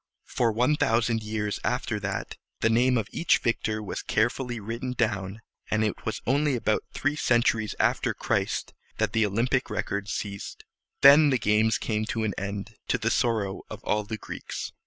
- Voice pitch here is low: Yes, low, 110 Hz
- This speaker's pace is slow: No, average, 175 wpm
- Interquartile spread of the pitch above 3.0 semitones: No, narrow, 2.4 semitones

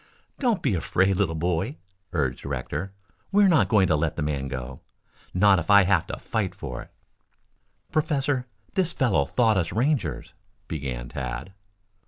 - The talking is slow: No, average, 160 wpm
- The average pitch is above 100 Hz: No, very low, 90 Hz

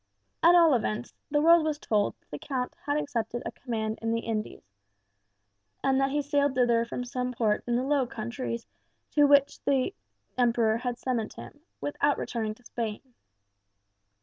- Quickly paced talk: No, average, 170 wpm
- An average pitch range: Yes, average, 3.7 semitones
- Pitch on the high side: Yes, very high, 250 Hz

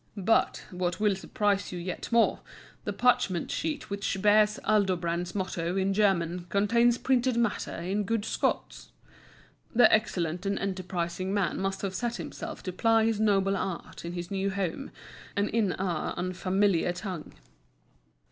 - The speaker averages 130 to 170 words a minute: Yes, average, 145 wpm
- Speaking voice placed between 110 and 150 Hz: No, high, 195 Hz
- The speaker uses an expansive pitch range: No, average, 2.9 semitones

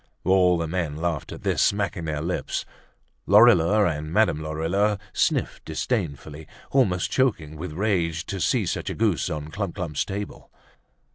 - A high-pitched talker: No, very low, 85 Hz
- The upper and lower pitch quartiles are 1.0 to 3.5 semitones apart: No, average, 4.3 semitones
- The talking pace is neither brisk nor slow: Yes, average, 150 wpm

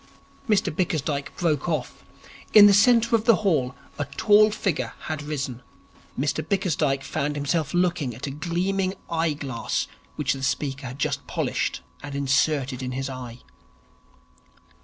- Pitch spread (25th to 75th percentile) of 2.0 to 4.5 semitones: No, average, 5.0 semitones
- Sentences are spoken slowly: No, average, 145 wpm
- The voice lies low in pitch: No, medium, 150 Hz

